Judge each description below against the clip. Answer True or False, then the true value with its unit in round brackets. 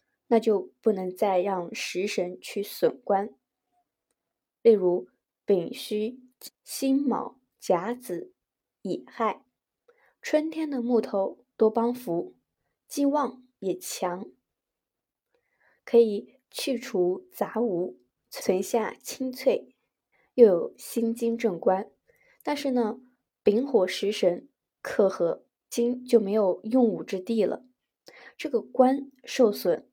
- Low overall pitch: False (230 Hz)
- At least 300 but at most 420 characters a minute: False (145 characters per minute)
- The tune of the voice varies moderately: True (4.8 semitones)